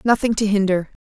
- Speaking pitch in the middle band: No, high, 205 Hz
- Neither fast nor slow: Yes, average, 175 wpm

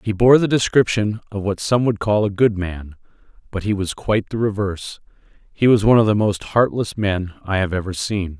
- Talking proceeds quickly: Yes, fast, 215 wpm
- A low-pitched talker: Yes, low, 100 Hz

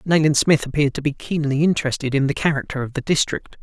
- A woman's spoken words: No, male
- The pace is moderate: No, fast, 215 wpm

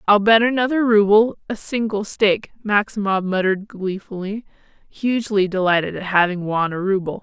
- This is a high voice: Yes, high, 205 Hz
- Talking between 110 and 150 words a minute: Yes, average, 140 wpm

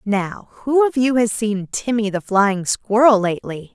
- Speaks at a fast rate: No, average, 175 wpm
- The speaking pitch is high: Yes, high, 215 Hz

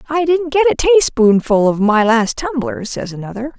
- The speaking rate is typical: Yes, average, 185 wpm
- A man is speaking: No, female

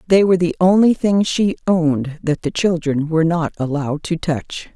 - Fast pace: No, average, 190 wpm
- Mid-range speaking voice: Yes, medium, 165 Hz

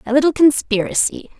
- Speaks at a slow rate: Yes, slow, 130 wpm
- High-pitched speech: Yes, very high, 270 Hz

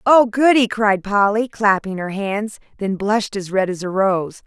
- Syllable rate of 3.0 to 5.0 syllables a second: Yes, 4.3 syllables/s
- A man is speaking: No, female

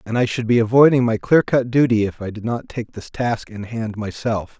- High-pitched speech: No, low, 115 Hz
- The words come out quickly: Yes, fast, 250 wpm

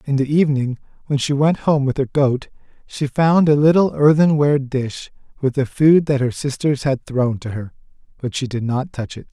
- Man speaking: Yes, male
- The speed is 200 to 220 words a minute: Yes, fast, 205 wpm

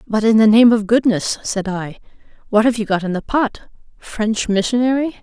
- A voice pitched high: Yes, high, 220 Hz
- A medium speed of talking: Yes, average, 195 wpm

